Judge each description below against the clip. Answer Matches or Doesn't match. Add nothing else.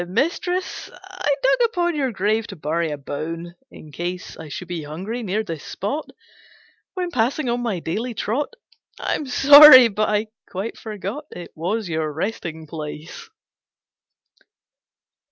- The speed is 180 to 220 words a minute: Doesn't match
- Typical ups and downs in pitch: Doesn't match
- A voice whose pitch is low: Doesn't match